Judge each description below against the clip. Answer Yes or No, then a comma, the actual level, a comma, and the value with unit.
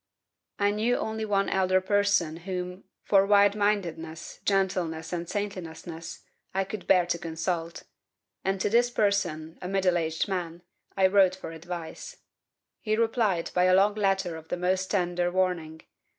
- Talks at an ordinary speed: Yes, average, 150 wpm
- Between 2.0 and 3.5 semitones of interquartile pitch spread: Yes, average, 2.9 semitones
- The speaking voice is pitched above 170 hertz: Yes, medium, 185 Hz